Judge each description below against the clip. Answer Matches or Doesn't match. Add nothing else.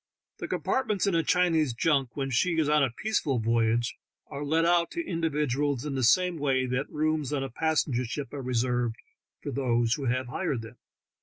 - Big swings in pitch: Doesn't match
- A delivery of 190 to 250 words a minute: Matches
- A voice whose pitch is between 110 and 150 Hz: Matches